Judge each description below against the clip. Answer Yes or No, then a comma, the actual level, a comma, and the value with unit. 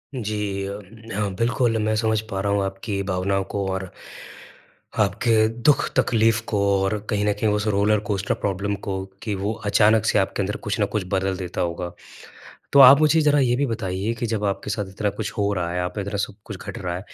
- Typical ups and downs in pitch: No, narrow, 2.3 semitones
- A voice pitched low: Yes, low, 105 Hz